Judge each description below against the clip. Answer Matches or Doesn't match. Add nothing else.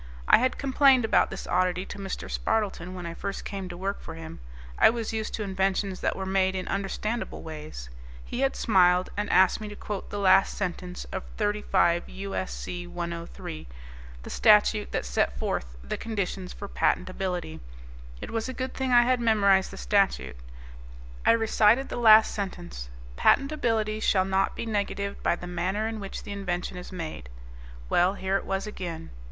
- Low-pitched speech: Doesn't match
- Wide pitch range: Doesn't match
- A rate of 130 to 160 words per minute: Doesn't match